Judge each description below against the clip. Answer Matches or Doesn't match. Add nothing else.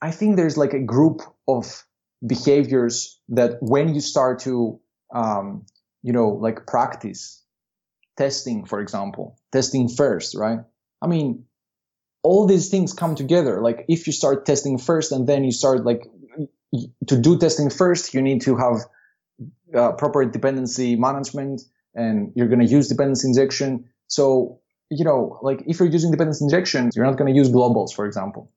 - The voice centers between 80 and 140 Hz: Matches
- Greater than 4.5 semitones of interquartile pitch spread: Doesn't match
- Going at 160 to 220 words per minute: Matches